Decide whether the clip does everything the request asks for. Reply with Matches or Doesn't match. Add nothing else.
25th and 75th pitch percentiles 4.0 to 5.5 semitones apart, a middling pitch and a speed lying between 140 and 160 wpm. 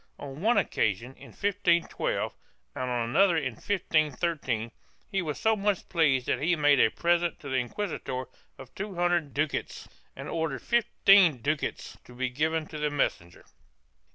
Matches